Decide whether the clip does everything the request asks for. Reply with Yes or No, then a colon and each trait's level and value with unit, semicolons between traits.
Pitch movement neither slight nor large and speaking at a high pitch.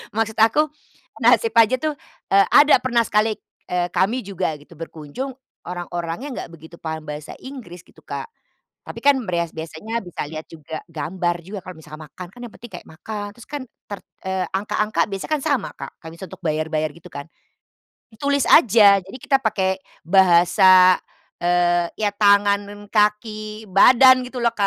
Yes: average, 4.6 semitones; high, 195 Hz